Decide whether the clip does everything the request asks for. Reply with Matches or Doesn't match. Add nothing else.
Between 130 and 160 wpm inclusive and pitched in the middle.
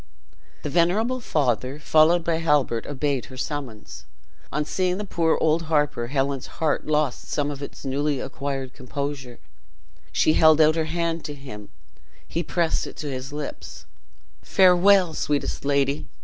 Matches